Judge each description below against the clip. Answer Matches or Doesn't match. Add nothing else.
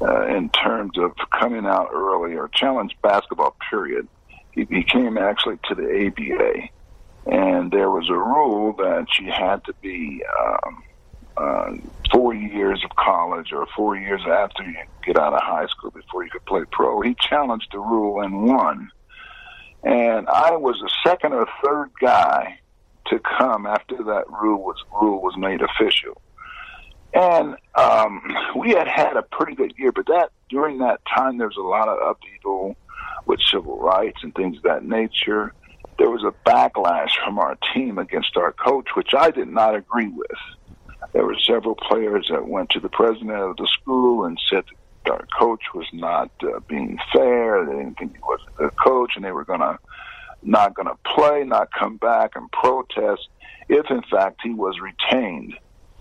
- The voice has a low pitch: Doesn't match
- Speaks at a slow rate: Doesn't match